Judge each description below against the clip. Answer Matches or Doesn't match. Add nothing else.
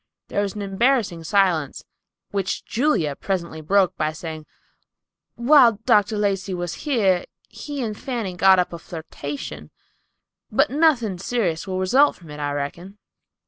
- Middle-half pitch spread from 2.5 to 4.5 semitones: Doesn't match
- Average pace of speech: Matches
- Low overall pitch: Doesn't match